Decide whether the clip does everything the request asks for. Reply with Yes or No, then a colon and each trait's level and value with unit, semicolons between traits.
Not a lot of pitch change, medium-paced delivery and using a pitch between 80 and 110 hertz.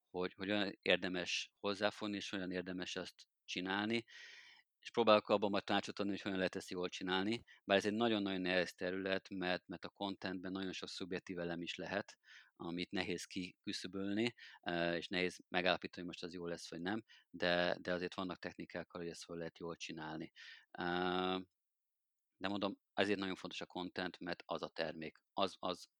No: narrow, 2.0 semitones; fast, 170 wpm; very low, 95 Hz